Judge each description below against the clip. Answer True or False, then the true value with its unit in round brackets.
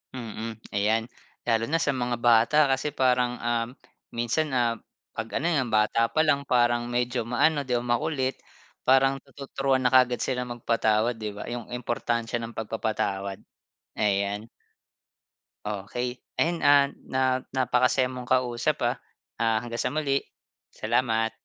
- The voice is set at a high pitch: False (120 Hz)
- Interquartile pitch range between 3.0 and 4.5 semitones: False (2.4 semitones)